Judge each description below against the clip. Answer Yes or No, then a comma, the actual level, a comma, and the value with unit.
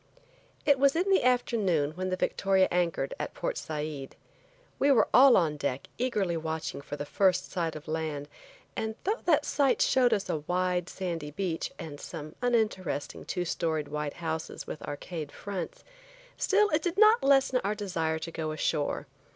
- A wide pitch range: Yes, wide, 7.5 semitones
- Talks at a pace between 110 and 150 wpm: No, average, 170 wpm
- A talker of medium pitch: Yes, medium, 180 Hz